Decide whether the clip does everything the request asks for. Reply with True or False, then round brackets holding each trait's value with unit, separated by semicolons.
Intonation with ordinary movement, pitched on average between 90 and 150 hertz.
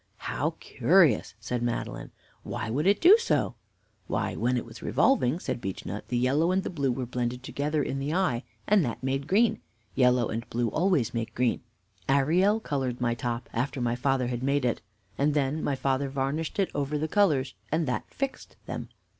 True (4.0 semitones; 135 Hz)